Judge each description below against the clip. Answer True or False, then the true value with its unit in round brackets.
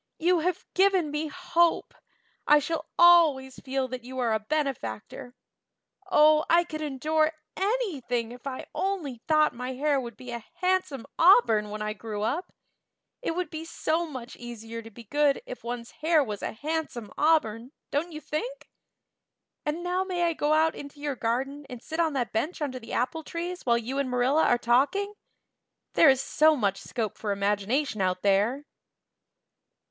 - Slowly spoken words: False (175 wpm)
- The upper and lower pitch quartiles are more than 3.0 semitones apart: True (5.3 semitones)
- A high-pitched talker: True (280 Hz)